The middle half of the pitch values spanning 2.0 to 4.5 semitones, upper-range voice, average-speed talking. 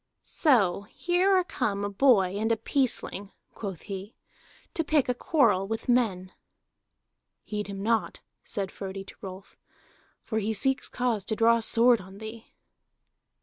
Yes: average, 3.8 semitones; high, 220 Hz; average, 145 wpm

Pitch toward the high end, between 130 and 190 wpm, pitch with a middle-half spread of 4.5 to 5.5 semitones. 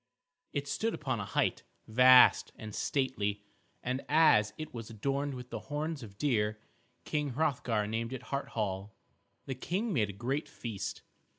No: low, 125 Hz; average, 160 wpm; average, 4.9 semitones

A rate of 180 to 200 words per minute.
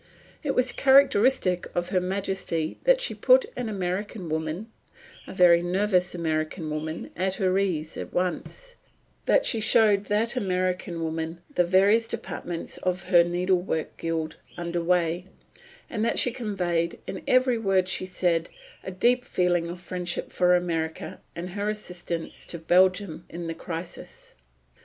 No: average, 145 wpm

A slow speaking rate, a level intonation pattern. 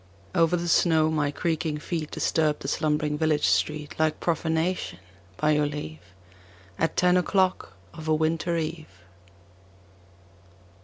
Yes: slow, 125 wpm; narrow, 1.8 semitones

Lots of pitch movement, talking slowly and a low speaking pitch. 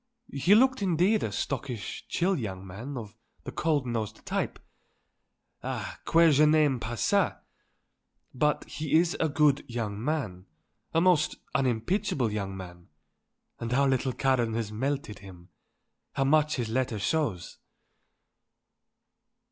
Yes: wide, 5.8 semitones; slow, 130 wpm; low, 130 Hz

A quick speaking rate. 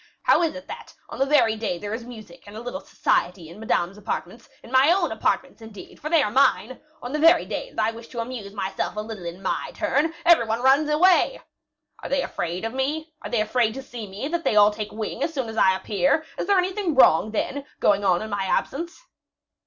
Yes: fast, 220 wpm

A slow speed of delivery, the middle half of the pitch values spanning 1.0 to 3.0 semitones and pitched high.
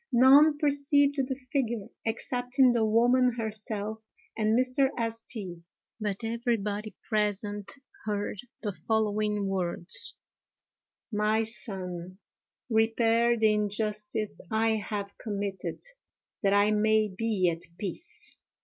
Yes: slow, 105 wpm; narrow, 2.5 semitones; high, 220 Hz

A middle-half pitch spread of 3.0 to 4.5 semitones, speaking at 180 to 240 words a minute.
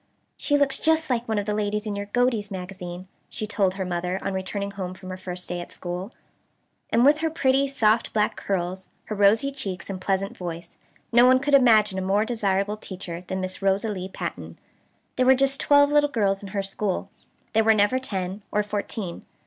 Yes: average, 4.1 semitones; fast, 205 wpm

